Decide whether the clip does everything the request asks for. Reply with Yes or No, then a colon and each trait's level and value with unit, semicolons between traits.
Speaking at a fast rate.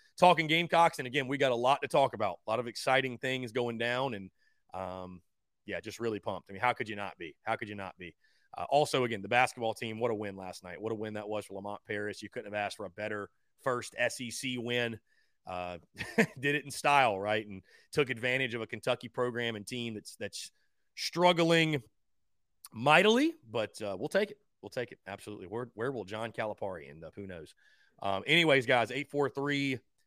Yes: fast, 215 wpm